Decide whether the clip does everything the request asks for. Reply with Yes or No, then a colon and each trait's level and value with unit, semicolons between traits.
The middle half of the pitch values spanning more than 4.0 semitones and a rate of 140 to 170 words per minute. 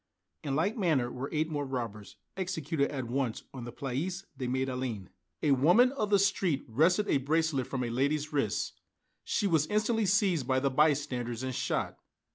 No: average, 5.2 semitones; average, 180 wpm